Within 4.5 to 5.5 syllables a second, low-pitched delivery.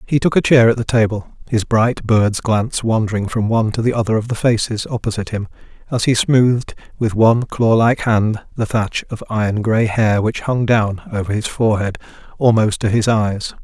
Yes: 5.3 syllables/s; low, 110 Hz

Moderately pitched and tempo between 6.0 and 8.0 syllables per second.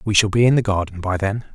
No: low, 100 Hz; 6.3 syllables/s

